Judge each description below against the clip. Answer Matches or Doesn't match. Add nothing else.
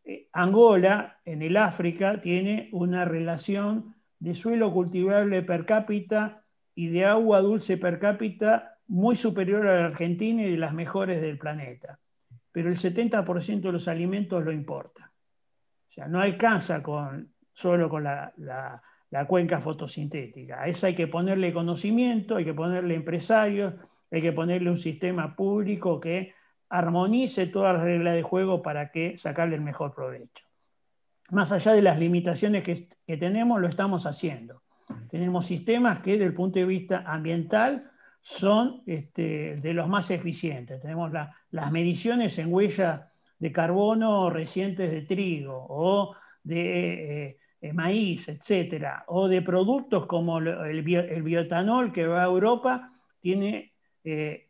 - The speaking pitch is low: Doesn't match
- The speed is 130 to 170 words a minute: Matches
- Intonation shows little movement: Doesn't match